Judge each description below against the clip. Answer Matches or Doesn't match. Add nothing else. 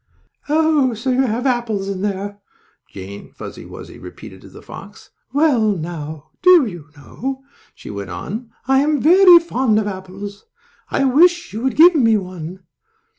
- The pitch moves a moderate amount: Doesn't match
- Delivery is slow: Doesn't match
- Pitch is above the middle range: Matches